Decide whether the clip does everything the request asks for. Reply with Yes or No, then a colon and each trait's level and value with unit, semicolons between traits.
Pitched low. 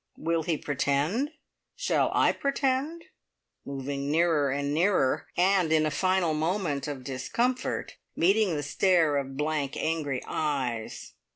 No: medium, 155 Hz